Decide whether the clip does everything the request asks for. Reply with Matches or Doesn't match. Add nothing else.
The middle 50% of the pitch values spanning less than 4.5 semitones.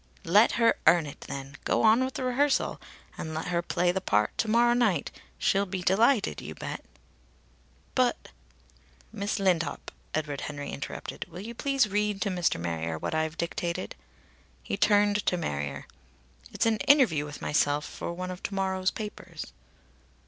Doesn't match